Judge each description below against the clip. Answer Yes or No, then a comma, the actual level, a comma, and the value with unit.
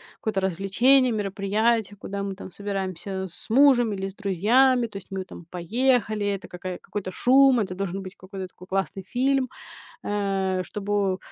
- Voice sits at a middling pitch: No, high, 200 Hz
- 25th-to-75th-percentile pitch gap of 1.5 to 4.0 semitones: Yes, average, 3.2 semitones